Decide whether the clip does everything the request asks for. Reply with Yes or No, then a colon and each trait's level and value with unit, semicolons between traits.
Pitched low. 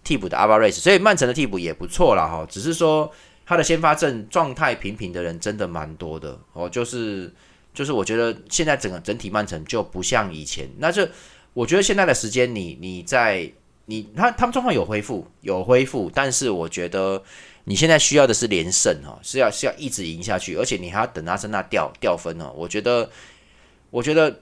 Yes: low, 110 Hz